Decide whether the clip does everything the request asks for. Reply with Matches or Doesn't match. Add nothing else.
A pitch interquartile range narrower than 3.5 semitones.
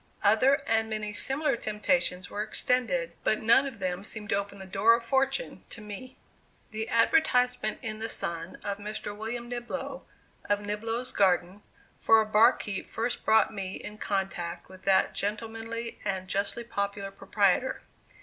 Matches